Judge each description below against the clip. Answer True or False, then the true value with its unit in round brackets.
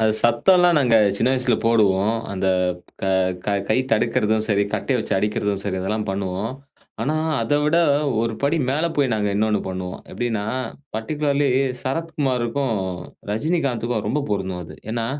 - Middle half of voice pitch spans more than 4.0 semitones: True (4.9 semitones)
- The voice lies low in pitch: True (115 Hz)